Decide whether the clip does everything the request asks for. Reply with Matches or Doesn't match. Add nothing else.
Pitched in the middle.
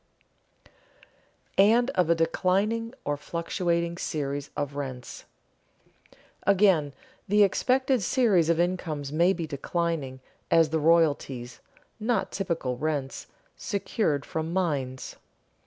Matches